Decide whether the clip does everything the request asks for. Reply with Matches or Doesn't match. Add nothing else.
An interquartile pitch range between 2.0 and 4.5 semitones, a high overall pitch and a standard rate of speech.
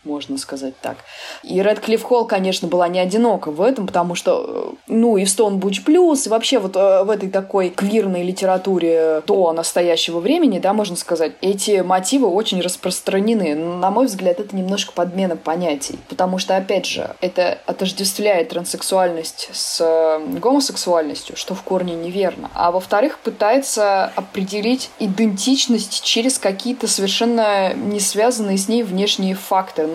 Matches